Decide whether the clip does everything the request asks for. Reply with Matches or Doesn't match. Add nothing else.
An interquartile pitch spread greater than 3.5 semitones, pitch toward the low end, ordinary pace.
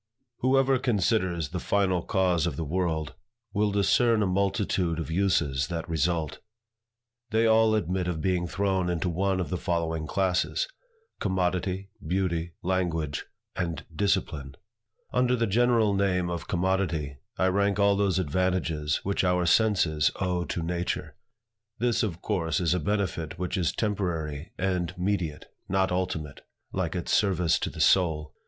Doesn't match